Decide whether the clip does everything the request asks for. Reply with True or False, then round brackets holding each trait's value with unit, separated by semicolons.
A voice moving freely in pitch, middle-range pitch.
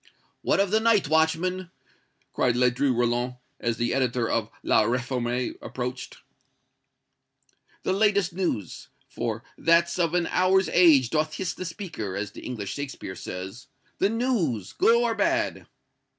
True (7.5 semitones; 150 Hz)